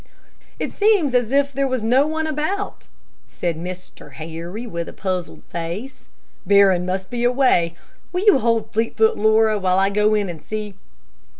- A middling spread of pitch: No, wide, 6.2 semitones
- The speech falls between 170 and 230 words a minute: No, average, 160 wpm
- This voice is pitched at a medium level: No, high, 215 Hz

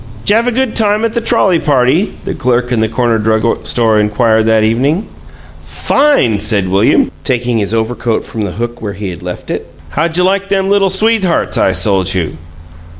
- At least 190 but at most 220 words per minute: Yes, average, 195 wpm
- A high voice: No, low, 120 Hz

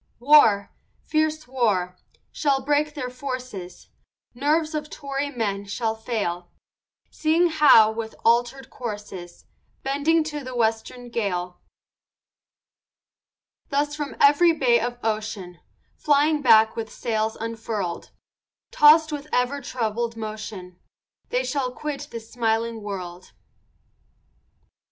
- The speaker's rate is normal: No, slow, 110 wpm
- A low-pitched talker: No, high, 240 Hz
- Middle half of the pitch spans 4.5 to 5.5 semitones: Yes, average, 4.9 semitones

